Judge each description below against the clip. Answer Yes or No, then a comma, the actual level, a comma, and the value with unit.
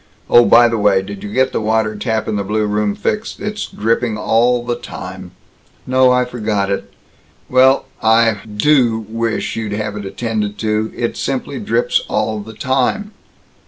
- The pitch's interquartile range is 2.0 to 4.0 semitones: Yes, narrow, 2.6 semitones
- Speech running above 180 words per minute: No, average, 170 wpm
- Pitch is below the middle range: Yes, low, 110 Hz